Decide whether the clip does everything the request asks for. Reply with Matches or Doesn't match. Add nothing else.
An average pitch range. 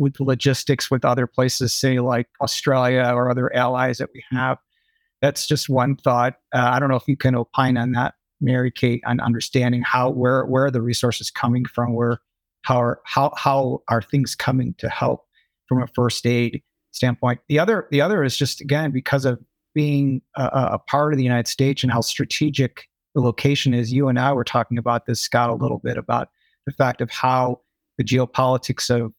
Doesn't match